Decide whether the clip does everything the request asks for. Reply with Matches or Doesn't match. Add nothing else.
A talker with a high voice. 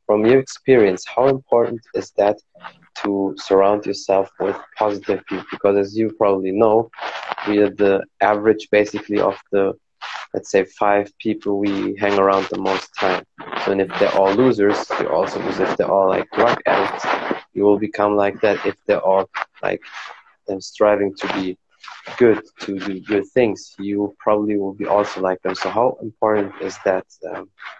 Doesn't match